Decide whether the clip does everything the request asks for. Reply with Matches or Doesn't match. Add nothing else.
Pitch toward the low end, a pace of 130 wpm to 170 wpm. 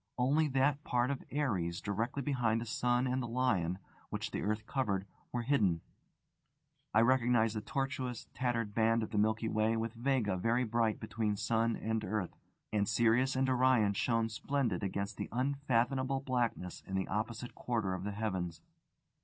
Matches